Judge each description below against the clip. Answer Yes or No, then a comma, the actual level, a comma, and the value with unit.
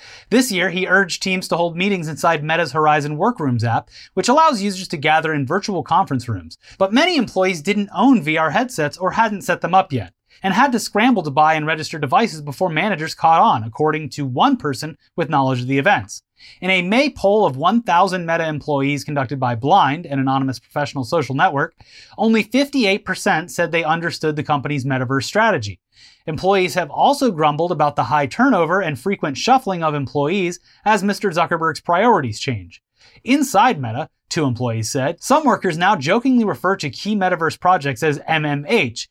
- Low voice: No, medium, 165 Hz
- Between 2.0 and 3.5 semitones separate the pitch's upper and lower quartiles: No, average, 5.2 semitones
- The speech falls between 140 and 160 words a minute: No, average, 180 wpm